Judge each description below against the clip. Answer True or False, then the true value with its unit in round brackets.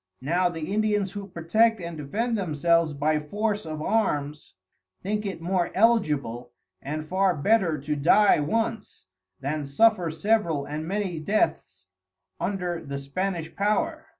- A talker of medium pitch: True (175 Hz)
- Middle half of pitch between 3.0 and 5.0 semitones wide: False (5.5 semitones)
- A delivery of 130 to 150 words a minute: True (135 wpm)